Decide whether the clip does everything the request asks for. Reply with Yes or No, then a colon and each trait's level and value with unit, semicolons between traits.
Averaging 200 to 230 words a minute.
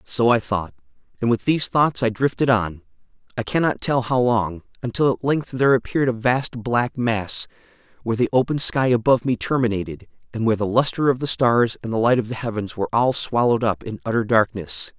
Yes: fast, 205 wpm